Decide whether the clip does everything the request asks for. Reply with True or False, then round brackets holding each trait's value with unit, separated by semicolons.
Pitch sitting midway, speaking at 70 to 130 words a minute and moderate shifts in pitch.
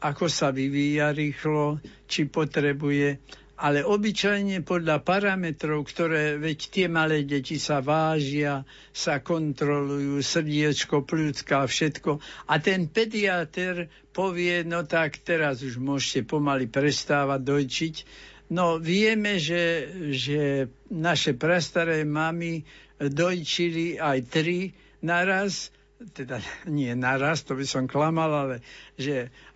True (155 Hz; 110 wpm; 3.3 semitones)